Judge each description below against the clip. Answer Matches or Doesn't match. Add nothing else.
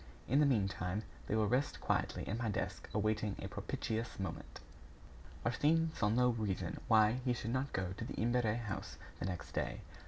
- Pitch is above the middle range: Doesn't match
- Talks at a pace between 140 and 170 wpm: Doesn't match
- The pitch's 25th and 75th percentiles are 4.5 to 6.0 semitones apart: Doesn't match